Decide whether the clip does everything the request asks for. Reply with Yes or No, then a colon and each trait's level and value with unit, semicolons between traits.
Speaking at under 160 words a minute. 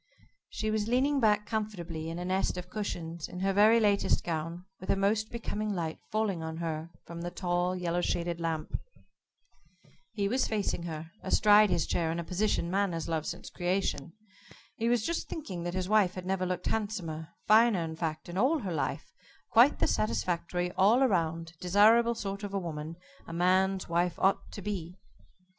No: average, 185 wpm